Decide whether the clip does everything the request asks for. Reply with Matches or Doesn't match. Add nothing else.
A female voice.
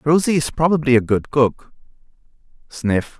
Doesn't match